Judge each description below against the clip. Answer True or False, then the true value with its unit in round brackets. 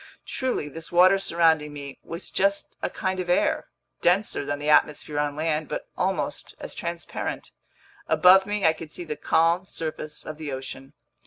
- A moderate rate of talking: True (170 wpm)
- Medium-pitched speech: True (160 Hz)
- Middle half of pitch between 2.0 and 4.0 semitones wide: True (3.3 semitones)